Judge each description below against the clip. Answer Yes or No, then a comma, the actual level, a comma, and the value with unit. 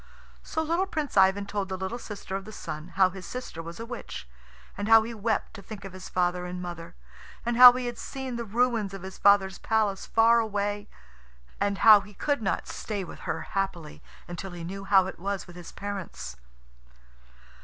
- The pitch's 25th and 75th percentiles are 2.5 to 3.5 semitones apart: Yes, average, 3.2 semitones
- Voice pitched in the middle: No, high, 200 Hz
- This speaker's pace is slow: No, average, 200 wpm